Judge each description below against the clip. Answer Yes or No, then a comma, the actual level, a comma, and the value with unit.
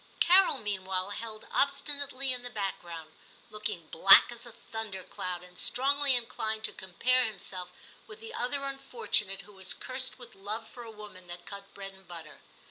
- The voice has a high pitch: Yes, high, 215 Hz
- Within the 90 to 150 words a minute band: No, average, 170 wpm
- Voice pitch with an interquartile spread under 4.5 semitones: No, average, 5.0 semitones